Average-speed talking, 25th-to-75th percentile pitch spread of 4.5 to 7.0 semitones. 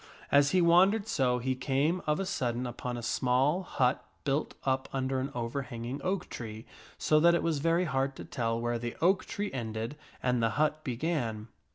Yes: average, 190 wpm; average, 4.9 semitones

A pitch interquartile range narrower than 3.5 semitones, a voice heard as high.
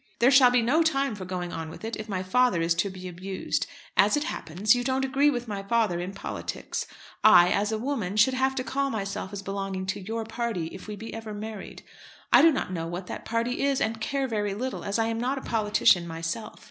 No: average, 4.8 semitones; high, 215 Hz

